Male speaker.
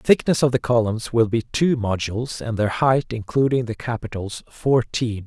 Yes: male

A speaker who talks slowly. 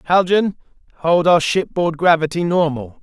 Yes: slow, 120 wpm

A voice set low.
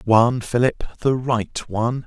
Yes: low, 120 Hz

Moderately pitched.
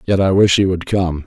No: very low, 90 Hz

